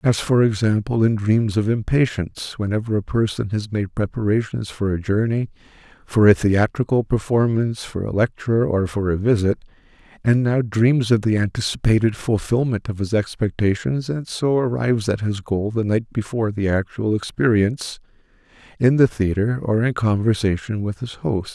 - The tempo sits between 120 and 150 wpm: No, average, 160 wpm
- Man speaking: Yes, male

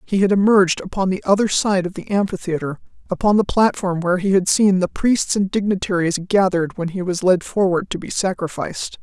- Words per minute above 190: Yes, average, 200 wpm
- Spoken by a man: No, female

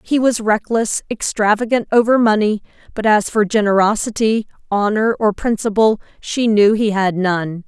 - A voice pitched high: Yes, high, 215 Hz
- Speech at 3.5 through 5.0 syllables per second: Yes, 4.6 syllables/s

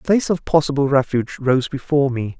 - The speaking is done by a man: Yes, male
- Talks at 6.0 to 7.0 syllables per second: Yes, 6.4 syllables/s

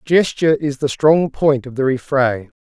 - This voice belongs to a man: Yes, male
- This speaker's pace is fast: No, average, 185 wpm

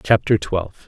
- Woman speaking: No, male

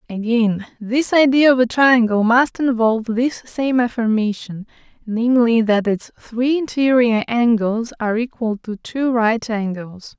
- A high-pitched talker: Yes, high, 235 Hz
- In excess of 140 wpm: No, slow, 135 wpm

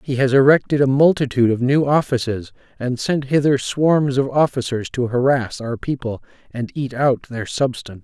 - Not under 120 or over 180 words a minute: Yes, average, 170 wpm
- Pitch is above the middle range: No, low, 130 Hz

